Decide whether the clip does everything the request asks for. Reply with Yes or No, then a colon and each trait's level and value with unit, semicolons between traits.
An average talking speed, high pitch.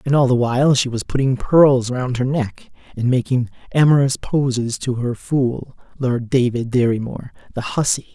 No: average, 175 wpm; low, 125 Hz